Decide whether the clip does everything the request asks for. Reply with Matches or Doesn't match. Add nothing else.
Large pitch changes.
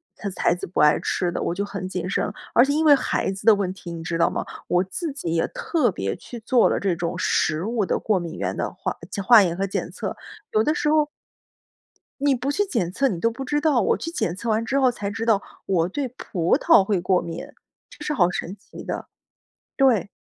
Matches